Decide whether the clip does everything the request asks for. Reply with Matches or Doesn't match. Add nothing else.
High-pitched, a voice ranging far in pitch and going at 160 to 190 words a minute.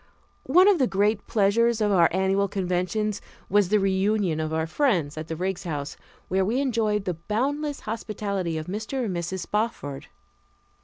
Doesn't match